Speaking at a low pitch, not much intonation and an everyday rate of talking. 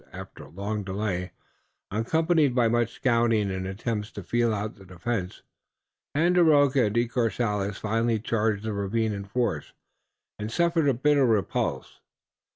No: low, 115 Hz; average, 3.3 semitones; average, 145 wpm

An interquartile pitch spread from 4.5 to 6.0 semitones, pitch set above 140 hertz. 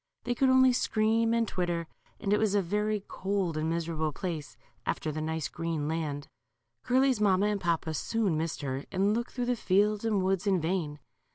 Yes: average, 5.1 semitones; medium, 185 Hz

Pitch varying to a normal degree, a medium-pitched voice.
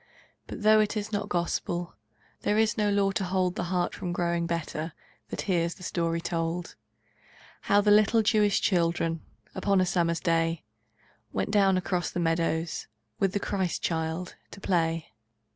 Yes: average, 3.1 semitones; medium, 175 Hz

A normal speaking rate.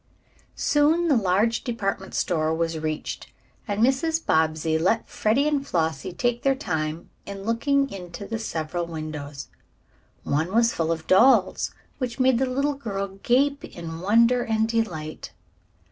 Yes: average, 145 wpm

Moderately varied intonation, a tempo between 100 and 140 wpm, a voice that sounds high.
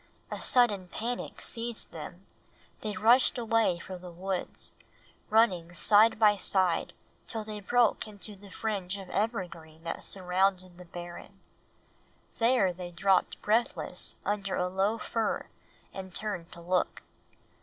Yes: average, 3.4 semitones; slow, 135 wpm; high, 195 Hz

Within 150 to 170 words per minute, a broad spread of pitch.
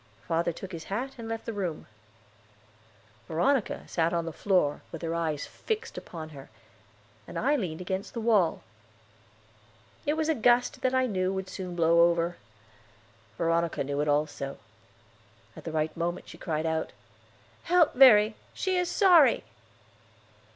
Yes: average, 155 wpm; wide, 6.4 semitones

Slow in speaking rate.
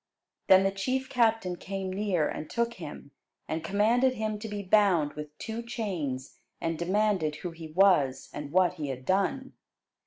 No: average, 165 wpm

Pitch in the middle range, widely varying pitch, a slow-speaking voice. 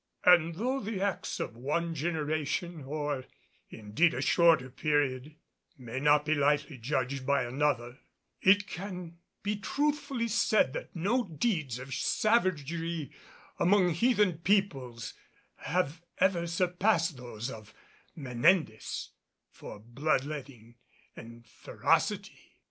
Yes: medium, 155 Hz; wide, 5.7 semitones; slow, 115 wpm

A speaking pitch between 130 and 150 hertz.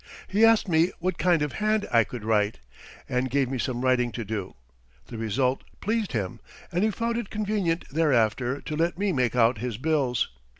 Yes: low, 135 Hz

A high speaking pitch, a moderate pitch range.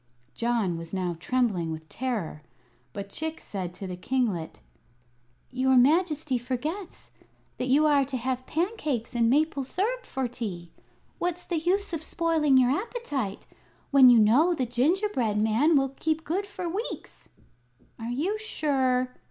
No: very high, 260 Hz; wide, 5.9 semitones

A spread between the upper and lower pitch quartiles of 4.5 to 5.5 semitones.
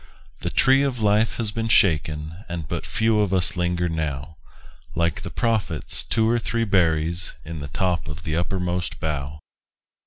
Yes: average, 5.2 semitones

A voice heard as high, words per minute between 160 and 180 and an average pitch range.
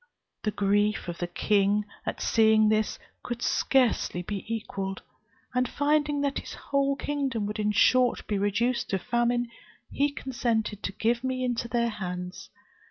Yes: high, 225 Hz; average, 165 wpm; average, 3.6 semitones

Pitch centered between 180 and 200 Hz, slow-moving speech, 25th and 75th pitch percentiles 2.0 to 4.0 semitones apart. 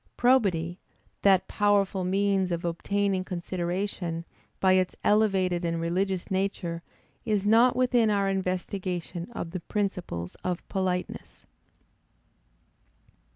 Yes: high, 190 Hz; slow, 105 wpm; narrow, 2.5 semitones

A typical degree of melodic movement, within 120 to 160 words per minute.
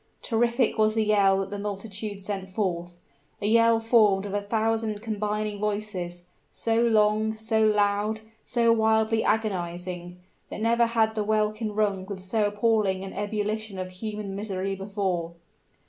No: narrow, 2.1 semitones; average, 145 wpm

